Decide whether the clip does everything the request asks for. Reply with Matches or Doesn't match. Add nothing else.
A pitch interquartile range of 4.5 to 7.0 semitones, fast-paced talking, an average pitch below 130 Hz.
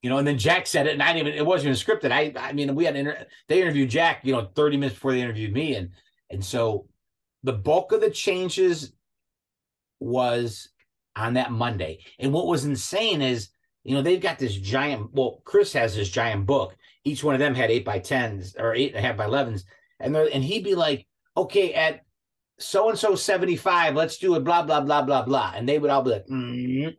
Doesn't match